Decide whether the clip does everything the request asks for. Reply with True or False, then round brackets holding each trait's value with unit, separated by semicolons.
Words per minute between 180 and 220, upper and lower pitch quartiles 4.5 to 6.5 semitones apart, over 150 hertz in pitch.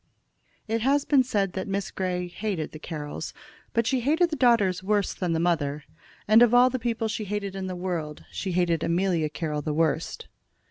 True (195 wpm; 5.3 semitones; 190 Hz)